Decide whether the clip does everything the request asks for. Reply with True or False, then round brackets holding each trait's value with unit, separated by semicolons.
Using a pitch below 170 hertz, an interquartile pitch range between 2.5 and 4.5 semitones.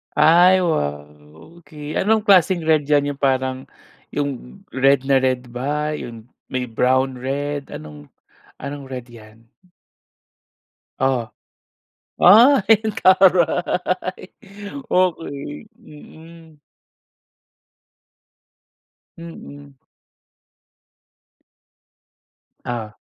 False (140 Hz; 5.1 semitones)